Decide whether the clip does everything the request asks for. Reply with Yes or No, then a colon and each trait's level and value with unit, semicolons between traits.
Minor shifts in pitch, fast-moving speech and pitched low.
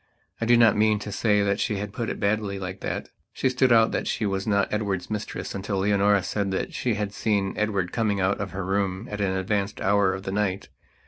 Yes: narrow, 1.7 semitones; fast, 230 wpm; low, 100 Hz